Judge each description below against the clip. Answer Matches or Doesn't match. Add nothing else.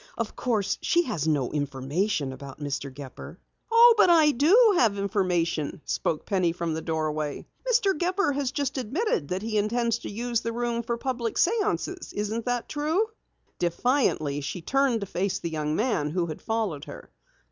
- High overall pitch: Matches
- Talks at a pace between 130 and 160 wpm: Doesn't match